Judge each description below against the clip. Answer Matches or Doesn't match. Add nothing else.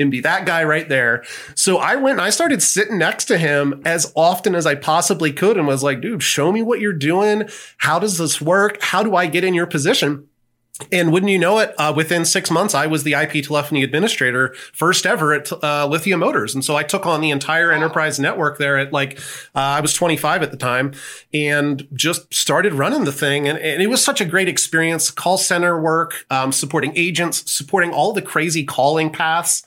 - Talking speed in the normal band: Doesn't match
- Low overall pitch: Doesn't match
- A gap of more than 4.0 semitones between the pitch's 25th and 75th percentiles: Doesn't match